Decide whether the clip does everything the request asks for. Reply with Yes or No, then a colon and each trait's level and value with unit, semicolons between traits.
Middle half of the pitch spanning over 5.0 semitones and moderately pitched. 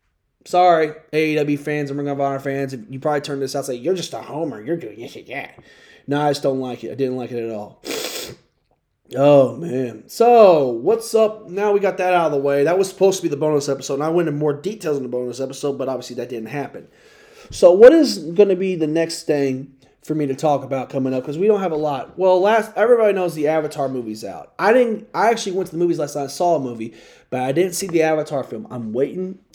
Yes: wide, 5.4 semitones; medium, 150 Hz